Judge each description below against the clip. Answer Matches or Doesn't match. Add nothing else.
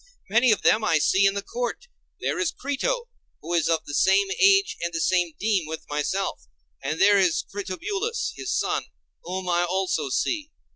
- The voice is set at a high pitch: Matches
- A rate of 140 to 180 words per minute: Doesn't match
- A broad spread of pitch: Matches